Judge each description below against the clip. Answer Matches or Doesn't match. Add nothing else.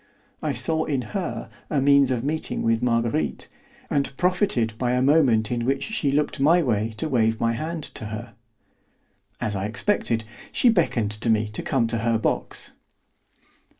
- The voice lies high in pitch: Doesn't match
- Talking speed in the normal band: Matches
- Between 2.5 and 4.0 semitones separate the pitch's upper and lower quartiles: Doesn't match